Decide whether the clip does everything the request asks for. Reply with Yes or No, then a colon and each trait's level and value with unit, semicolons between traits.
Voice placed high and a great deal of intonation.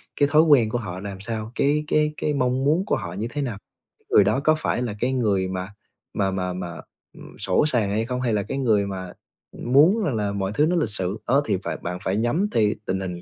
No: low, 115 Hz; wide, 6.2 semitones